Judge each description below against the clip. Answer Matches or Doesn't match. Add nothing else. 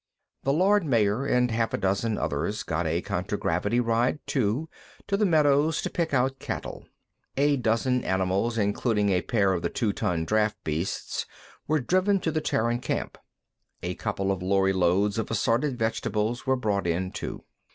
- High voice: Doesn't match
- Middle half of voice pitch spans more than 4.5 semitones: Matches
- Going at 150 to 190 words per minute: Matches